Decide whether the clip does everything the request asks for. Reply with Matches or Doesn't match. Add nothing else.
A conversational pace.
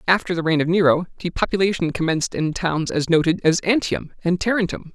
Matches